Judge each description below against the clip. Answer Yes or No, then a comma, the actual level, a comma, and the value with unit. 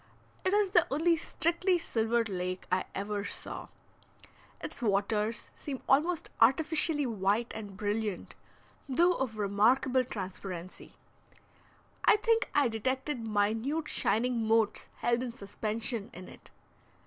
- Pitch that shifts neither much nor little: No, wide, 5.8 semitones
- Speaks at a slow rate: Yes, slow, 120 wpm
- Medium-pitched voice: No, high, 230 Hz